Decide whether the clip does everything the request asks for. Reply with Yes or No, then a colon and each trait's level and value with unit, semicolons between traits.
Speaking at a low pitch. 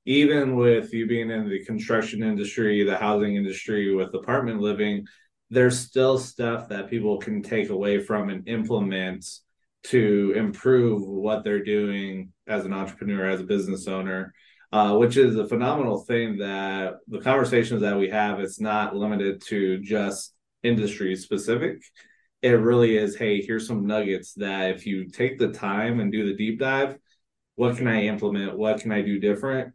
Yes: low, 105 Hz